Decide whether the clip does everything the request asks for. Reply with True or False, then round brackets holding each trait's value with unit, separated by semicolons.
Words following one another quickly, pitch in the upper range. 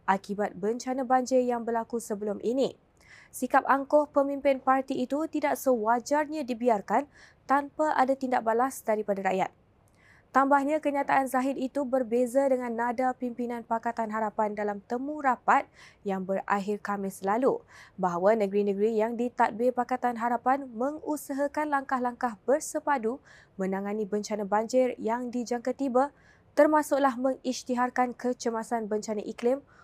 False (115 wpm; 245 Hz)